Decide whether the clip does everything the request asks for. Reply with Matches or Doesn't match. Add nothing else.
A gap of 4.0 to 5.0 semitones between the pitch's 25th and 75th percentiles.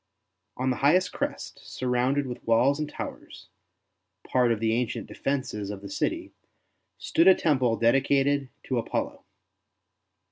Doesn't match